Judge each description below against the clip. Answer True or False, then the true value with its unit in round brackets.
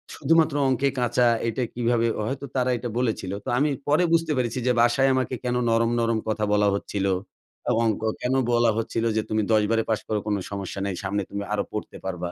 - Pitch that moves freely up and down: False (3.0 semitones)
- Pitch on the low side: True (115 Hz)